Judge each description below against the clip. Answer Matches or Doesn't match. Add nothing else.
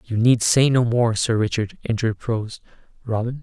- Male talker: Matches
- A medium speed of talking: Matches